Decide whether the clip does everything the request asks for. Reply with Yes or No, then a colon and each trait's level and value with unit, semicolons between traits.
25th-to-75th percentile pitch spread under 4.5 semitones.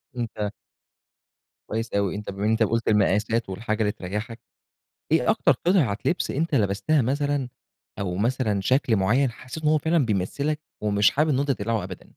No: average, 5.3 semitones